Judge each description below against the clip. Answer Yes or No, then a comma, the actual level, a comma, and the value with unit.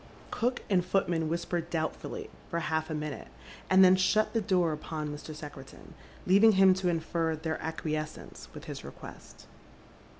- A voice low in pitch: No, medium, 165 Hz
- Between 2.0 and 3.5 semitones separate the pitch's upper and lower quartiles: Yes, average, 3.2 semitones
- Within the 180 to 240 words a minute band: No, average, 155 wpm